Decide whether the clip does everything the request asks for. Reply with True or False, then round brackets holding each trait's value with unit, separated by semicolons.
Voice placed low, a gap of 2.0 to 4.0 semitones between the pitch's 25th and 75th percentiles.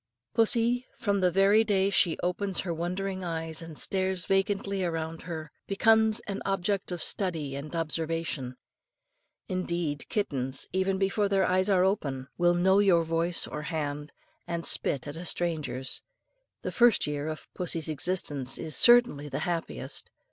False (175 Hz; 3.7 semitones)